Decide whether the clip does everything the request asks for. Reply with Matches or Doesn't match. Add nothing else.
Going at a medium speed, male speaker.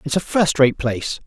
Doesn't match